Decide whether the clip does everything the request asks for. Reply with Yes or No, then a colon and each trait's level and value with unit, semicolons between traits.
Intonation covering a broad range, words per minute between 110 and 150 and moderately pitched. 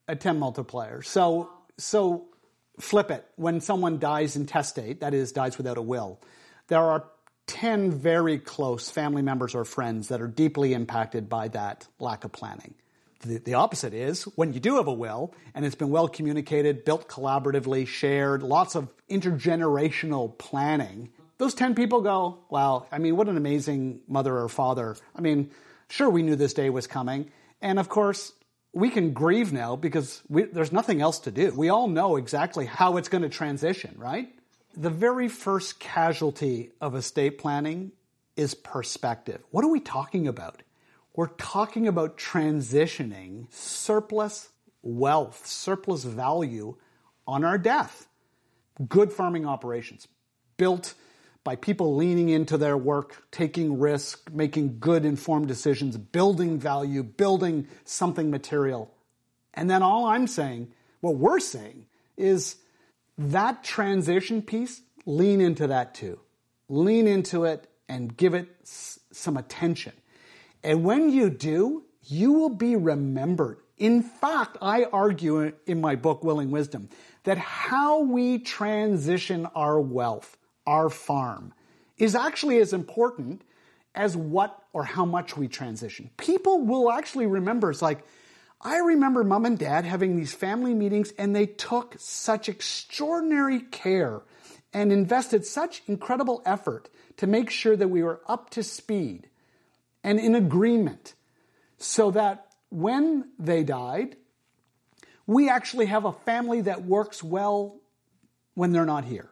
Yes: wide, 6.4 semitones; average, 145 wpm; medium, 165 Hz